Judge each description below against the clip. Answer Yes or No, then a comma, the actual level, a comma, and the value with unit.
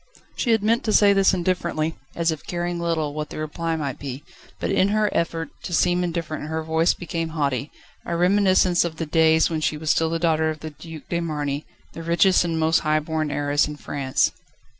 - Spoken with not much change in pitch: Yes, narrow, 2.1 semitones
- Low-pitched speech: No, medium, 165 Hz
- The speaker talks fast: Yes, fast, 210 wpm